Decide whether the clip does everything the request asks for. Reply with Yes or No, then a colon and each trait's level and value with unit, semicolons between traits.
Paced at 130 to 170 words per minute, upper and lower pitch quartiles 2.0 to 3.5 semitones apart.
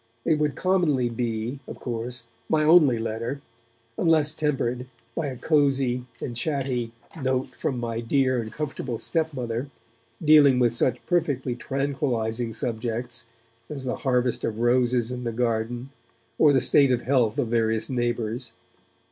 Yes: average, 140 wpm; average, 3.0 semitones